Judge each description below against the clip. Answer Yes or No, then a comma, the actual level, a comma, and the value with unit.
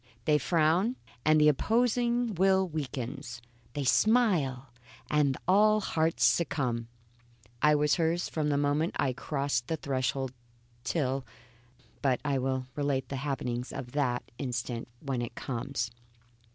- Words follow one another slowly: Yes, slow, 130 wpm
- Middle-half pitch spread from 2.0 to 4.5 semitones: Yes, average, 4.0 semitones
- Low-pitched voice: No, medium, 145 Hz